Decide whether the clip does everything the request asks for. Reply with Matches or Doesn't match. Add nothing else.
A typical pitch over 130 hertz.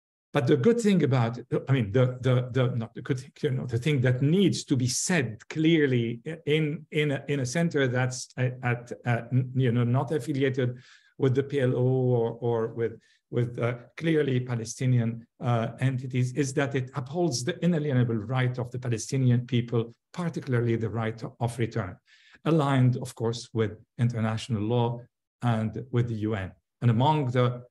Doesn't match